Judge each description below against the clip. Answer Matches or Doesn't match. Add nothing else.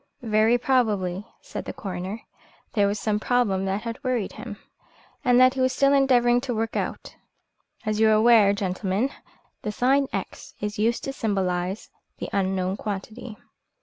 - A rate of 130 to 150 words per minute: Doesn't match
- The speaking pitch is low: Doesn't match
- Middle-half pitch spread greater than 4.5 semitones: Doesn't match